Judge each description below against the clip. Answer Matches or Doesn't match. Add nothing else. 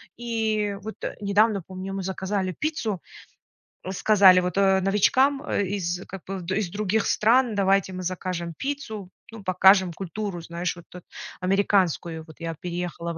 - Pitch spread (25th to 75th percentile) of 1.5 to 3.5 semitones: Matches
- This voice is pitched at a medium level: Doesn't match